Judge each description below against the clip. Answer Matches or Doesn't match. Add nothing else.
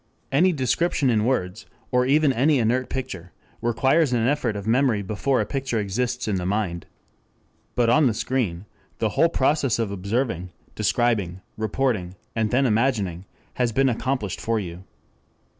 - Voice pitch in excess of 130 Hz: Doesn't match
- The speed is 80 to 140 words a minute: Doesn't match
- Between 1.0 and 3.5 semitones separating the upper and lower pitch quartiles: Doesn't match